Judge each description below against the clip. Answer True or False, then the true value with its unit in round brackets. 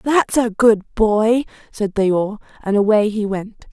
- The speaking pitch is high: True (215 Hz)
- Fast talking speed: False (175 wpm)